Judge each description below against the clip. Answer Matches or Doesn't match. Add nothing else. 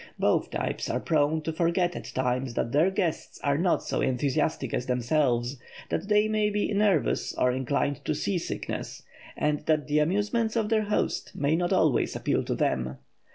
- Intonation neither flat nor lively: Doesn't match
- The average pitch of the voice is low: Doesn't match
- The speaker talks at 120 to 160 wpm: Doesn't match